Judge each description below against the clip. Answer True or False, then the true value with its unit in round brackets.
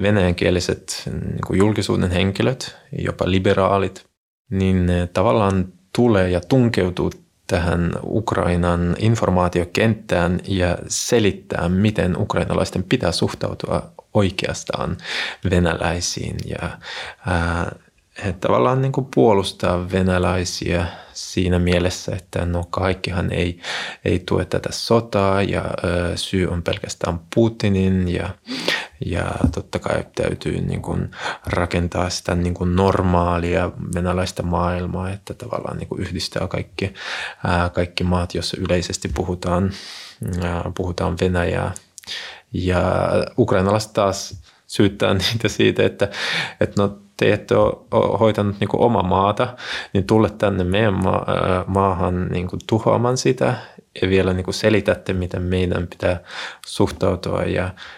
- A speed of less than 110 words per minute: False (115 wpm)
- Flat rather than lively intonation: True (2.0 semitones)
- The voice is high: False (95 Hz)